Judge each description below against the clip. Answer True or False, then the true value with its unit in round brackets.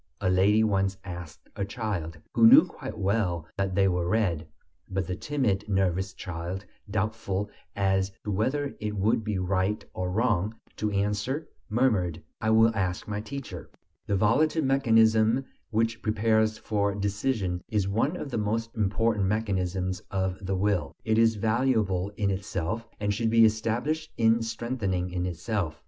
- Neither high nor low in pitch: False (105 Hz)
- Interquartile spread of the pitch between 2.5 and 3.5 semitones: True (3.0 semitones)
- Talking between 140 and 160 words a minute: True (155 wpm)